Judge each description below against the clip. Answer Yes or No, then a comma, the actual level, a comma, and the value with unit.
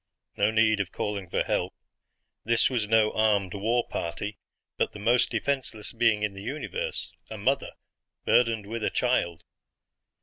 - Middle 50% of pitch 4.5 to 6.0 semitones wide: No, average, 2.7 semitones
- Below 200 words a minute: Yes, average, 155 wpm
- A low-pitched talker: Yes, low, 110 Hz